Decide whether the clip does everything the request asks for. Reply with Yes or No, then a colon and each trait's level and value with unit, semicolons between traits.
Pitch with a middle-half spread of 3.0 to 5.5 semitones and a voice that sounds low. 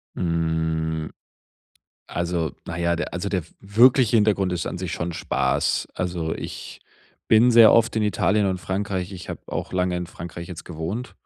Yes: average, 3.4 semitones; very low, 90 Hz